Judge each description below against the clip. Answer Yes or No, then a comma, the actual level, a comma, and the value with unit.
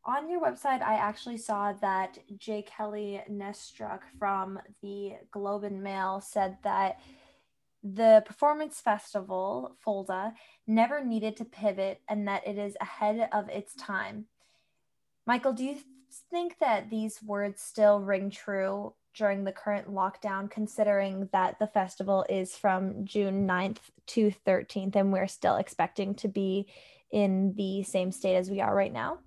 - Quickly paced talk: No, average, 150 wpm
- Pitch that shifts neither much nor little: No, narrow, 1.9 semitones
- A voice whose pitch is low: No, high, 205 Hz